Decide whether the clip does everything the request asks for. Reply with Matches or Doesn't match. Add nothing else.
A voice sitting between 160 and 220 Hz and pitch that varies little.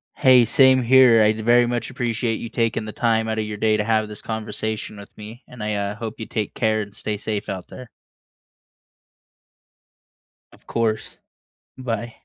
Doesn't match